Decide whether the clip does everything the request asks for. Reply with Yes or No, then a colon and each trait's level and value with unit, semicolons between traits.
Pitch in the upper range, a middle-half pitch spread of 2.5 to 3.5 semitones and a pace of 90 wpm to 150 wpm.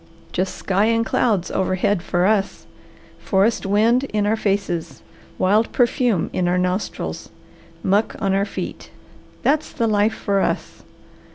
Yes: high, 205 Hz; average, 2.9 semitones; average, 140 wpm